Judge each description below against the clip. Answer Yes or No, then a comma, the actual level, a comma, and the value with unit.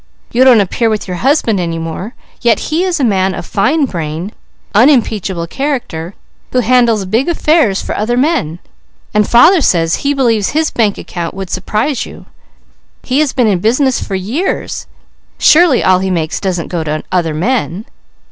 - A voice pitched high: Yes, high, 215 Hz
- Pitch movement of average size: No, wide, 6.3 semitones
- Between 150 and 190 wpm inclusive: Yes, average, 170 wpm